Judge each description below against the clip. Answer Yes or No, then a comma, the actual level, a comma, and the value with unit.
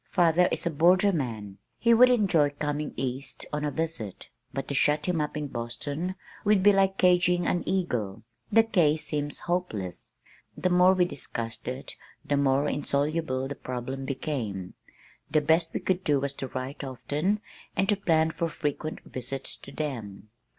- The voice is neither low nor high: Yes, medium, 150 Hz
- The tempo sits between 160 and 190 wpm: Yes, average, 165 wpm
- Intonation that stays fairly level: No, average, 5.0 semitones